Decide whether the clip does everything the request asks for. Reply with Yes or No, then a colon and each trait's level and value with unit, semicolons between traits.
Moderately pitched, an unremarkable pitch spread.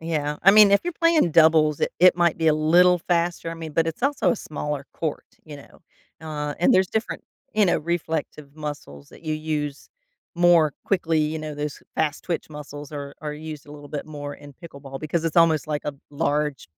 No: medium, 155 Hz; narrow, 2.3 semitones